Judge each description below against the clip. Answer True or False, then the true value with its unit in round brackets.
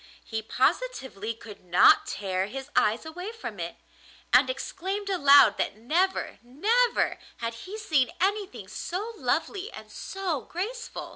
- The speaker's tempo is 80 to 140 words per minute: True (135 wpm)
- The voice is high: True (340 Hz)